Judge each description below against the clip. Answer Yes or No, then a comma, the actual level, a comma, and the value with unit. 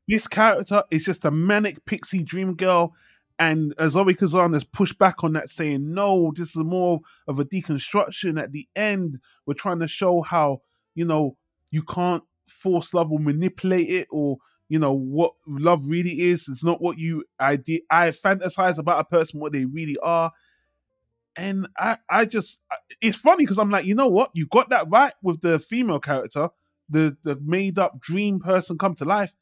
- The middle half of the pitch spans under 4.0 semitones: Yes, average, 3.6 semitones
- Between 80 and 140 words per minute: No, average, 185 wpm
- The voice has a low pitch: No, medium, 170 Hz